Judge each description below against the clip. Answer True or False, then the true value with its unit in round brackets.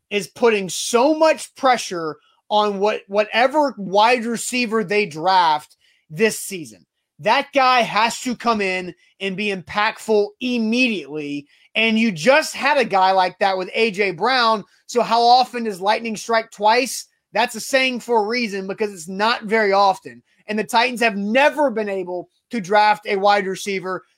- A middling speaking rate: True (160 wpm)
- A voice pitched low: False (215 Hz)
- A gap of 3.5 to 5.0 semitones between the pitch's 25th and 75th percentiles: False (3.1 semitones)